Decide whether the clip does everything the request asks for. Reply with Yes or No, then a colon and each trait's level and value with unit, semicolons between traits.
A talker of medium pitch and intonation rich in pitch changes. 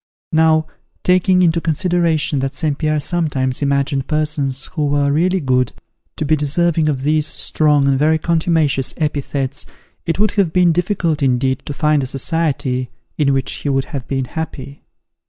No: medium, 150 Hz; average, 2.9 semitones